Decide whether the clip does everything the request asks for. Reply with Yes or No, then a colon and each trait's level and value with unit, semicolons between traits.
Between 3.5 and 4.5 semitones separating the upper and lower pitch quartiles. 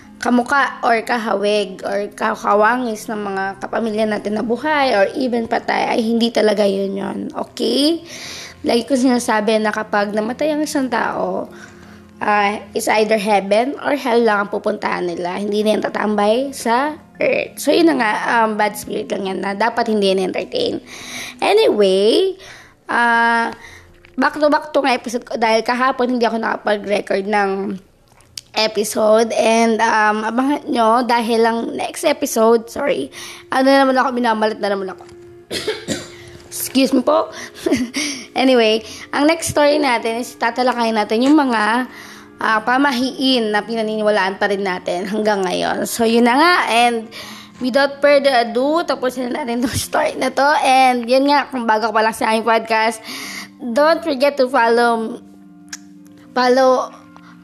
Yes: average, 3.8 semitones